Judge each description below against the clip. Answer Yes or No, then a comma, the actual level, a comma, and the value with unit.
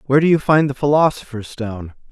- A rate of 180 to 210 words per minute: Yes, average, 200 wpm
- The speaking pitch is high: No, low, 135 Hz